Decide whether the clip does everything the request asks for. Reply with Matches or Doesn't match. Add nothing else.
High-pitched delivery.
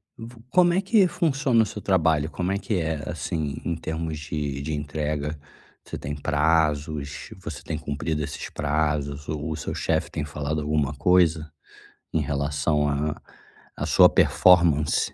Doesn't match